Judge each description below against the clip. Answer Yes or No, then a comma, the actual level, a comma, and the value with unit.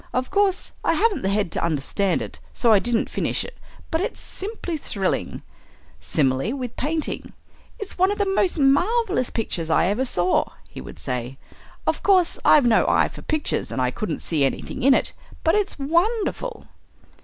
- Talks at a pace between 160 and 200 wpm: Yes, average, 180 wpm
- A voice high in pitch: Yes, very high, 270 Hz